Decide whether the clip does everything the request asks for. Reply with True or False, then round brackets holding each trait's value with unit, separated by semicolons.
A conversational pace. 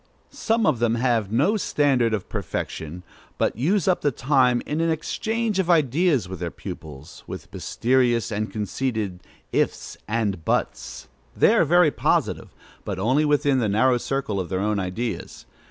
True (160 wpm)